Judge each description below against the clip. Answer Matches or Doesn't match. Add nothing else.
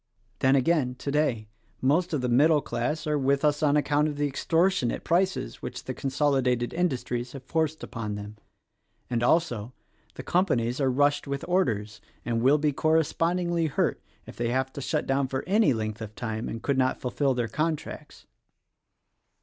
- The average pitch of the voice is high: Doesn't match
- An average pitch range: Matches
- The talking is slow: Doesn't match